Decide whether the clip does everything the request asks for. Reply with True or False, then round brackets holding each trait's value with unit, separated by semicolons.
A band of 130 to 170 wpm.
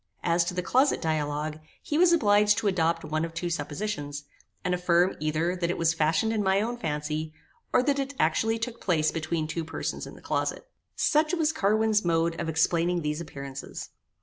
False (190 wpm)